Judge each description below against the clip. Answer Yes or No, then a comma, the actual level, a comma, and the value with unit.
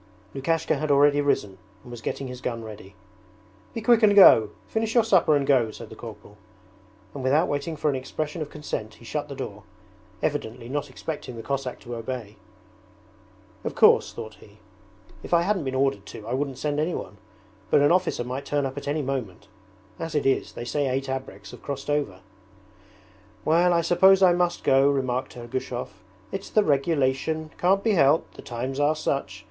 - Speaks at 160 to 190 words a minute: Yes, average, 185 wpm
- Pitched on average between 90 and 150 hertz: Yes, medium, 140 Hz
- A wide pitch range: No, average, 4.3 semitones